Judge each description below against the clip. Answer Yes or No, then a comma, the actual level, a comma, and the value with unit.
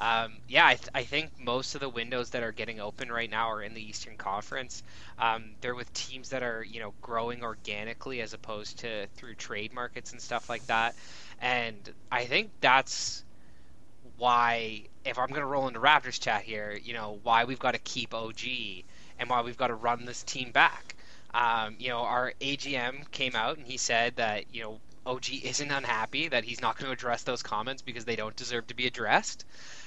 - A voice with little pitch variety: Yes, narrow, 2.2 semitones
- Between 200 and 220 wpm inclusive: Yes, fast, 205 wpm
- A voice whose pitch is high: No, low, 120 Hz